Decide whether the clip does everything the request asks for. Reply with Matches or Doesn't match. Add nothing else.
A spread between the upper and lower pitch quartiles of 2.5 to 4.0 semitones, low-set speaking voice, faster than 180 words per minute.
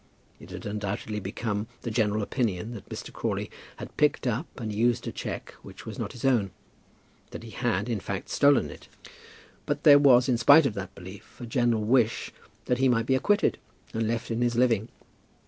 Matches